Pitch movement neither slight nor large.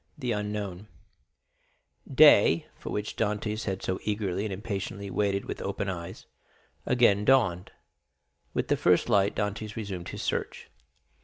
No: narrow, 1.9 semitones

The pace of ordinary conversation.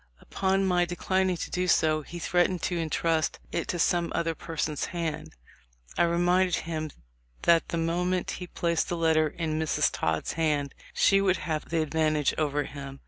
Yes: average, 170 wpm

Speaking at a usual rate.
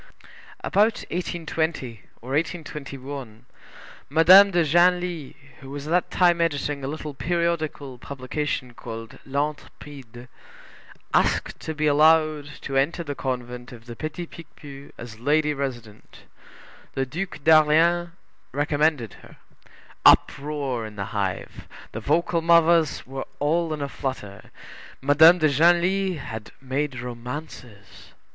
No: slow, 120 wpm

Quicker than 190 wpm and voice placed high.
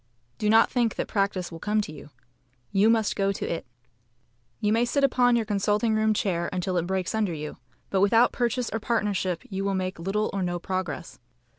Yes: average, 200 wpm; high, 200 Hz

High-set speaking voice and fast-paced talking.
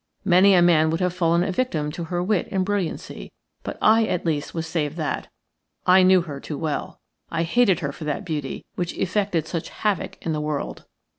No: medium, 170 Hz; fast, 210 wpm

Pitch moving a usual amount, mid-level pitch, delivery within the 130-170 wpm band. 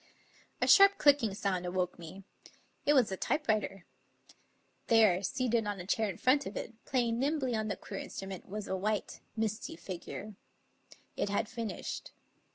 No: average, 3.7 semitones; high, 215 Hz; average, 160 wpm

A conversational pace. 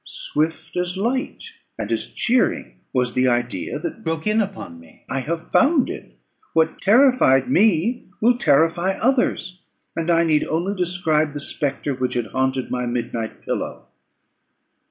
Yes: average, 150 wpm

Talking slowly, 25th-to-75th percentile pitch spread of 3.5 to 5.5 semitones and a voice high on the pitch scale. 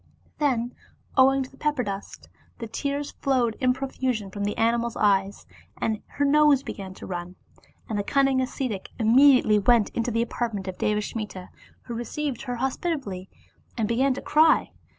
No: average, 170 wpm; average, 4.4 semitones; high, 235 Hz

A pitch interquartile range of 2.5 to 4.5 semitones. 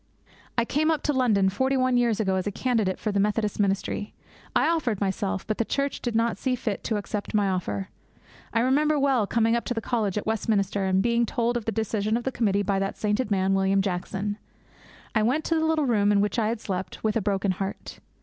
Yes: average, 3.3 semitones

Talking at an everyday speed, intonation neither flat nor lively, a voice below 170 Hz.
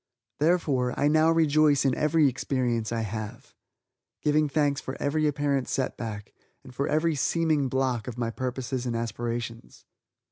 Yes: average, 150 wpm; average, 3.9 semitones; low, 135 Hz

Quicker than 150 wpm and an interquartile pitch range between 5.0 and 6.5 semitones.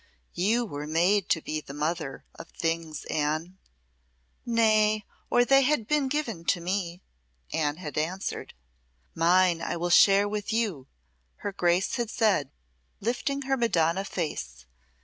No: average, 140 wpm; average, 5.3 semitones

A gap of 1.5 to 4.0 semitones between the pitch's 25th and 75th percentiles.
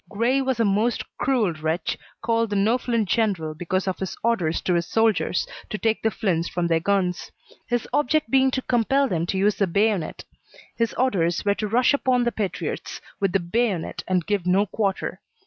No: average, 4.5 semitones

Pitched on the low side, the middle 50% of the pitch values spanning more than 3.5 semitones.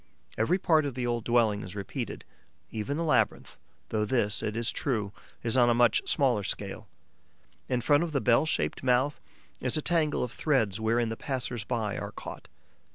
Yes: low, 120 Hz; average, 3.9 semitones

